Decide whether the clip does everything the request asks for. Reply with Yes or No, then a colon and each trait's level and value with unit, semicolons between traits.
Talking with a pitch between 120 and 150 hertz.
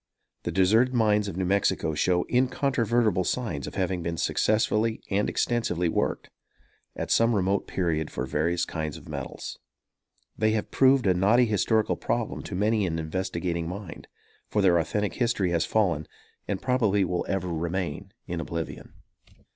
No: very low, 95 Hz